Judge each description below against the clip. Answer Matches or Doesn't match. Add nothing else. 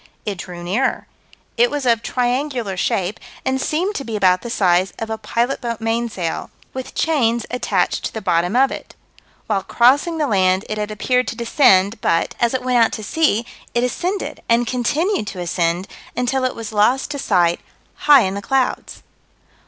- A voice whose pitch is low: Doesn't match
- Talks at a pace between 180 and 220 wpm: Matches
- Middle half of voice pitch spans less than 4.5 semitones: Doesn't match